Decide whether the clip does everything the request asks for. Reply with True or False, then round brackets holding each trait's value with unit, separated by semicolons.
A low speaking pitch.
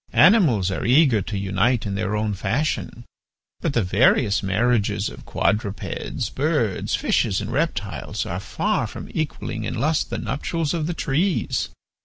True (115 Hz)